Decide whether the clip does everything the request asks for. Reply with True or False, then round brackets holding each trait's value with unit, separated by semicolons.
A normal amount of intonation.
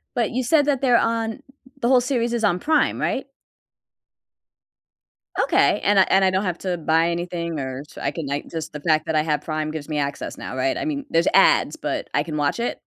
False (7.4 semitones)